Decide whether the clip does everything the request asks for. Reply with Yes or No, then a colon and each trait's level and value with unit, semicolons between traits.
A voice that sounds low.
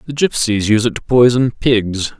Yes: low, 115 Hz